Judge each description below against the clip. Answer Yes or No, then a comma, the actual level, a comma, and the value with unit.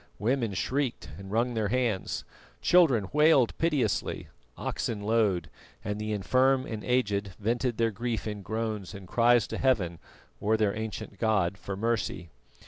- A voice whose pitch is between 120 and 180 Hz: No, low, 110 Hz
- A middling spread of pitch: Yes, average, 3.3 semitones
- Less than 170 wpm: Yes, average, 145 wpm